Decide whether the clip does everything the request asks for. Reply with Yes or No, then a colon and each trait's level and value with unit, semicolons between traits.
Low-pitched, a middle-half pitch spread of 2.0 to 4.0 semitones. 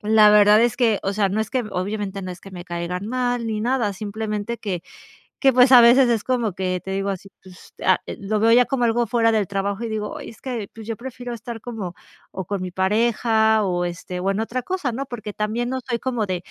No: high, 215 Hz; average, 3.4 semitones